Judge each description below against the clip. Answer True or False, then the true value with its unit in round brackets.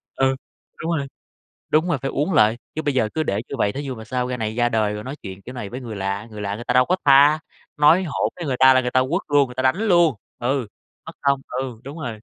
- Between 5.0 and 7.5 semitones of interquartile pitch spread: False (4.5 semitones)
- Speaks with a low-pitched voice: True (130 Hz)